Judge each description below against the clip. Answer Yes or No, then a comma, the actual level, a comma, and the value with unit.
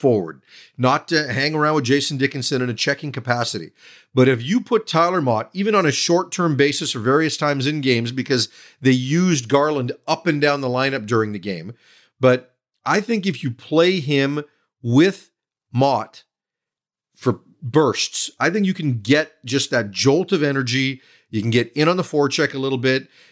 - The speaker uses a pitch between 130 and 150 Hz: Yes, medium, 140 Hz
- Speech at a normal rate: Yes, average, 185 wpm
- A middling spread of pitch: Yes, average, 3.6 semitones